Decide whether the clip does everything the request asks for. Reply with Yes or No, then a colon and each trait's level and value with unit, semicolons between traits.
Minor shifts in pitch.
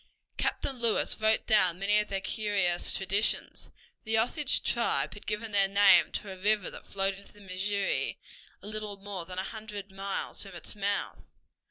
Yes: narrow, 1.8 semitones